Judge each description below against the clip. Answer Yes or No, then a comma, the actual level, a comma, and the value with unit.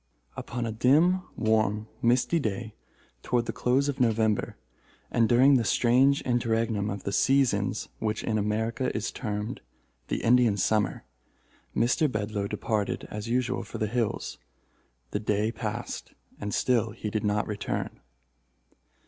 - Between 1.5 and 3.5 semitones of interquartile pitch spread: Yes, average, 2.8 semitones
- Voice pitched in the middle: No, low, 115 Hz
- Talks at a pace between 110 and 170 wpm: Yes, average, 140 wpm